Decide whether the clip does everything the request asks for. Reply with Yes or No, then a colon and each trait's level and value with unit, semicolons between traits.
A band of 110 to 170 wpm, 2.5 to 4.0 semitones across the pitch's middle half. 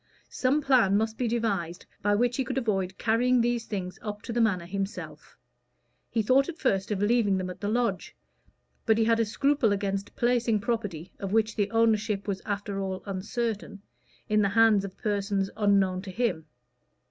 No: average, 180 wpm; average, 2.9 semitones